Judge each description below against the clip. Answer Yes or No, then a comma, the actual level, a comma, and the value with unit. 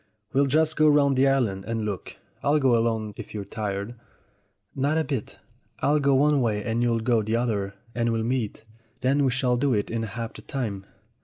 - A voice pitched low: Yes, low, 120 Hz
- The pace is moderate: No, fast, 210 wpm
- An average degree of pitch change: Yes, average, 3.9 semitones